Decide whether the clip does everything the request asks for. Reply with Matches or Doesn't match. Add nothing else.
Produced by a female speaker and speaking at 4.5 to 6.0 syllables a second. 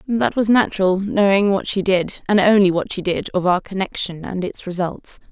Matches